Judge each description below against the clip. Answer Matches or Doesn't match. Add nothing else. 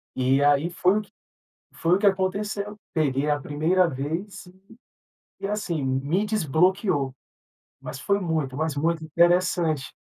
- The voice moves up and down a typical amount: Matches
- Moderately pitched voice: Matches